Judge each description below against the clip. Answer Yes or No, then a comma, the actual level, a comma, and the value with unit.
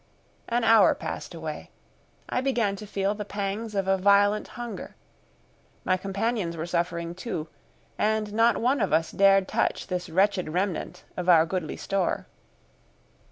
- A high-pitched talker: Yes, high, 195 Hz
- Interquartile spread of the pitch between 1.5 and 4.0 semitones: Yes, average, 3.0 semitones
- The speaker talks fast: No, average, 150 wpm